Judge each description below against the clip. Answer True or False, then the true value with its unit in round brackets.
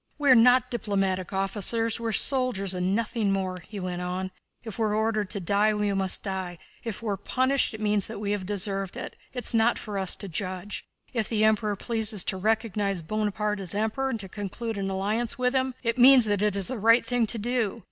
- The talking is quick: True (220 wpm)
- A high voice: True (210 Hz)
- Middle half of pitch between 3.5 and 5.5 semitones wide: False (2.9 semitones)